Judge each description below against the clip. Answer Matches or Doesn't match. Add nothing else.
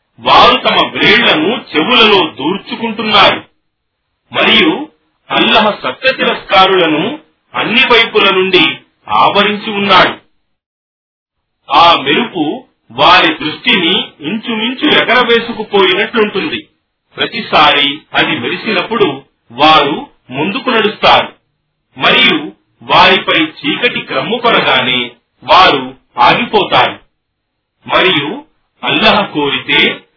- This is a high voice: Matches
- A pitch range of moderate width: Doesn't match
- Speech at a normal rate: Doesn't match